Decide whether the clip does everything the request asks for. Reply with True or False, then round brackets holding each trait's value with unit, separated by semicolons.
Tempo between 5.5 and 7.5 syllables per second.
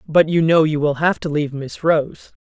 False (5.0 syllables/s)